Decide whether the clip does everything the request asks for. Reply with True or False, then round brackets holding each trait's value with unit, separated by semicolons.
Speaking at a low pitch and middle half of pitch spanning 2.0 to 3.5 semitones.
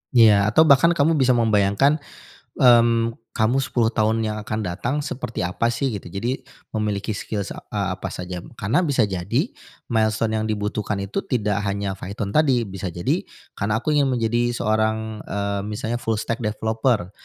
True (110 Hz; 2.8 semitones)